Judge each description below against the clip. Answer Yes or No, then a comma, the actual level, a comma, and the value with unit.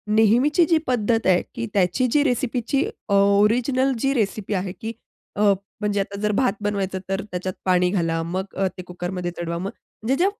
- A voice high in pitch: Yes, high, 205 Hz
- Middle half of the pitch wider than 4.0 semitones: Yes, average, 4.6 semitones